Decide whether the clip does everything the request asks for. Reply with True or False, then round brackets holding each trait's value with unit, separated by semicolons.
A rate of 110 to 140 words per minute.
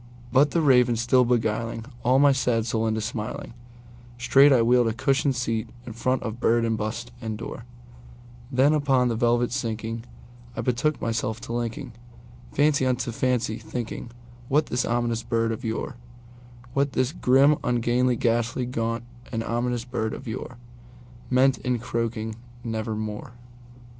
True (135 wpm)